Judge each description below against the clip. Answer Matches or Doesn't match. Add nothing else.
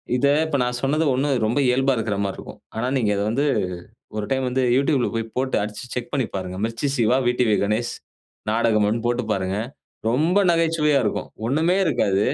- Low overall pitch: Matches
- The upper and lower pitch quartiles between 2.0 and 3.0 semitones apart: Doesn't match